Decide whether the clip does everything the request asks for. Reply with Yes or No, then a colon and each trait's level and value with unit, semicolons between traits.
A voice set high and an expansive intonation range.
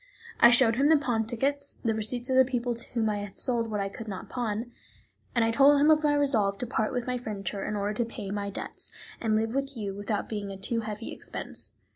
No: high, 230 Hz; average, 3.4 semitones